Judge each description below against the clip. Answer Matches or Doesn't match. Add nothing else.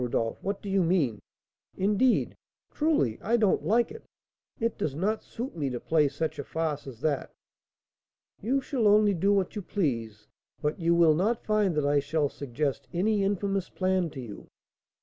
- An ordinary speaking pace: Matches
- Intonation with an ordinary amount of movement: Doesn't match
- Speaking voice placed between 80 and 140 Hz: Doesn't match